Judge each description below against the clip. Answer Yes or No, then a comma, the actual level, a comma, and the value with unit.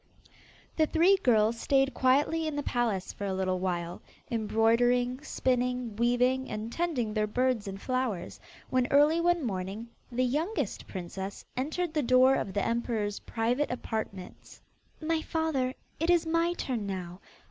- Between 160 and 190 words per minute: No, average, 145 wpm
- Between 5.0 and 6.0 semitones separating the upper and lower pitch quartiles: Yes, wide, 5.4 semitones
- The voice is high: Yes, high, 245 Hz